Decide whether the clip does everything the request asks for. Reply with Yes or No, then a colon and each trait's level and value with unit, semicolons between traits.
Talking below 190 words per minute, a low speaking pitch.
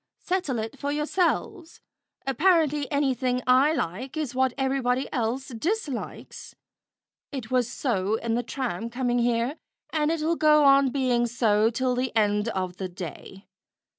No: average, 140 wpm; very high, 255 Hz